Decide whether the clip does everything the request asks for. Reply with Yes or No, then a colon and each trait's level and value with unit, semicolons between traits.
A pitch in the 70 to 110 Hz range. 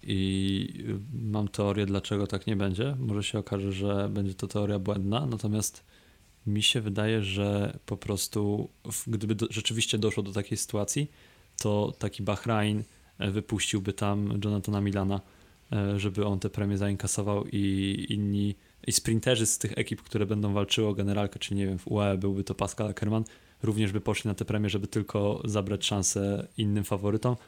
Yes: low, 105 Hz